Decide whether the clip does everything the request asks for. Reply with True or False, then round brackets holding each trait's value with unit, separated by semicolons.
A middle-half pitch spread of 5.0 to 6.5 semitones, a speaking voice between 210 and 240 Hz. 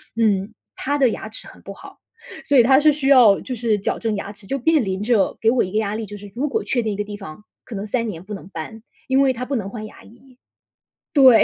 False (4.1 semitones; 225 Hz)